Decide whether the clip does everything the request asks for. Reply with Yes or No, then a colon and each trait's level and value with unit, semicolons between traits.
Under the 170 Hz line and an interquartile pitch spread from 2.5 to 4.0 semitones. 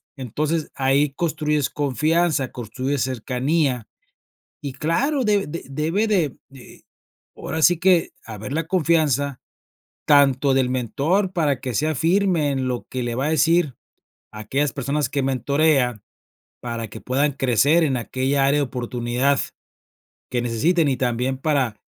Yes: medium, 140 Hz; average, 3.7 semitones